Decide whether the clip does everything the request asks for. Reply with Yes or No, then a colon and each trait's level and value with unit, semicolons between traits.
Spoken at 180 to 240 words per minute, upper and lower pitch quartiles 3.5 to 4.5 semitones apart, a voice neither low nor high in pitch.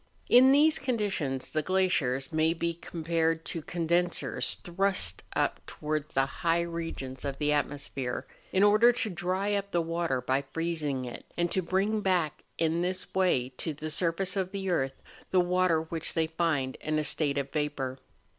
No: average, 170 wpm; average, 4.0 semitones; medium, 165 Hz